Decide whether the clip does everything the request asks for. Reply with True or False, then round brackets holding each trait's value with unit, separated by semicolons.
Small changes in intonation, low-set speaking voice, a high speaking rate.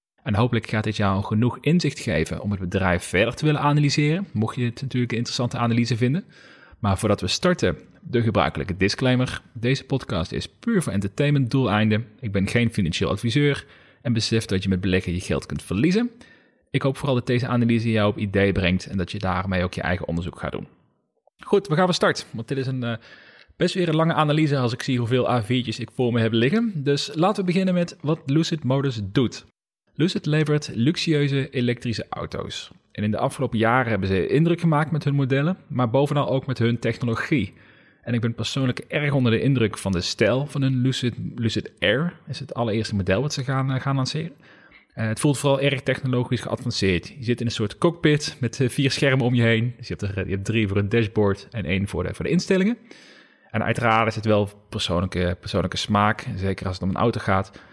False (5.3 semitones; 120 Hz; 215 wpm)